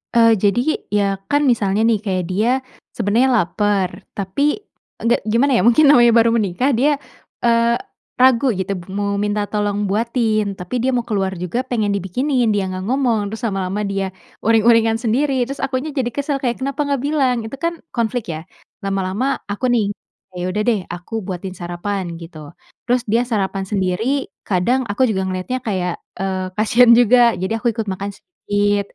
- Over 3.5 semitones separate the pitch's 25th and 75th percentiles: Yes, average, 4.1 semitones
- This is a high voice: Yes, high, 215 Hz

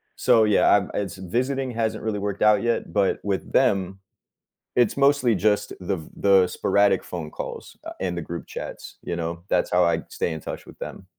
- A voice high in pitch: No, low, 100 Hz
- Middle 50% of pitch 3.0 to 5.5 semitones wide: Yes, average, 3.5 semitones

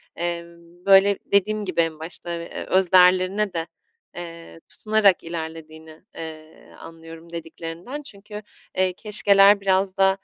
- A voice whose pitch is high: No, medium, 180 Hz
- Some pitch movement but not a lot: Yes, average, 3.1 semitones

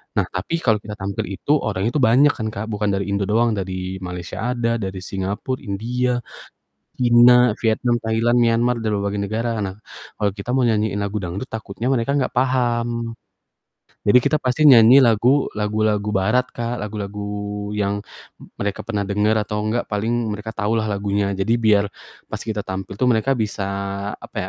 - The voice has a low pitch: Yes, low, 110 Hz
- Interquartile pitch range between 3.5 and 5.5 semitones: No, average, 2.8 semitones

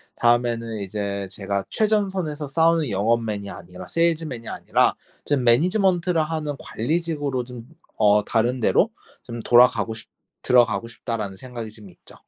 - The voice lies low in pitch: Yes, low, 120 Hz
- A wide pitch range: Yes, wide, 6.3 semitones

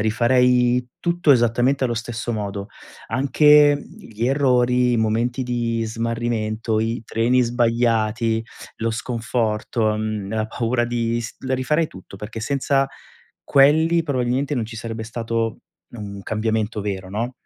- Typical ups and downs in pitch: No, narrow, 2.2 semitones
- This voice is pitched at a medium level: No, low, 115 Hz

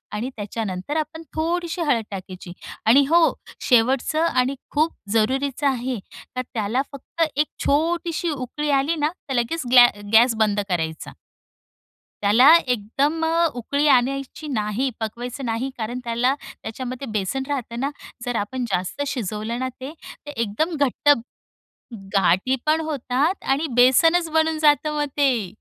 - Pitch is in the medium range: No, very high, 260 Hz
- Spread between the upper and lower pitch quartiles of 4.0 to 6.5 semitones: Yes, average, 4.7 semitones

